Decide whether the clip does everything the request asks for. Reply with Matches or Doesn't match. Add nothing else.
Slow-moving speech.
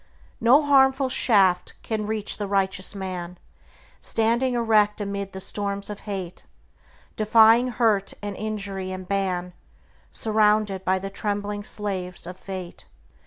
Matches